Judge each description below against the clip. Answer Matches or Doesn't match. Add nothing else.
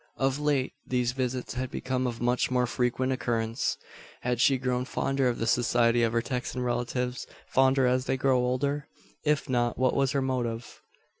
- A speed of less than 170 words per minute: Doesn't match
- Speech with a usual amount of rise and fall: Doesn't match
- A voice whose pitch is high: Doesn't match